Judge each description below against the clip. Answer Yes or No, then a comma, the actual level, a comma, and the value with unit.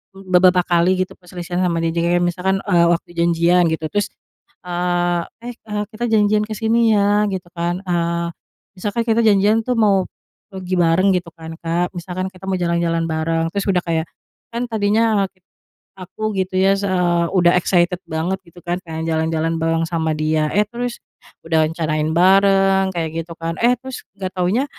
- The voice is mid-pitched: Yes, medium, 180 Hz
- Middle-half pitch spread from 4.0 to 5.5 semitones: No, average, 2.9 semitones